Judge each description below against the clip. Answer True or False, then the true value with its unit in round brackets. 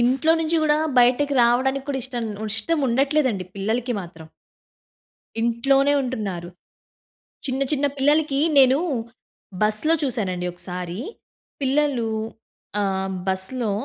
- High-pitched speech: True (250 Hz)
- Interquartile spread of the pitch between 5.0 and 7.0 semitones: True (5.3 semitones)